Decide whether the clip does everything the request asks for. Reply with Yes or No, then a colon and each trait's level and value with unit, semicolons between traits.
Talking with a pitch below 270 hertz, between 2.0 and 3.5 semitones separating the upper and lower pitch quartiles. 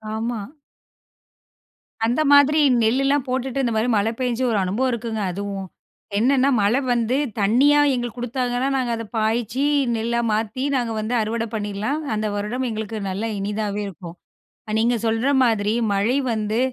Yes: high, 230 Hz; average, 3.0 semitones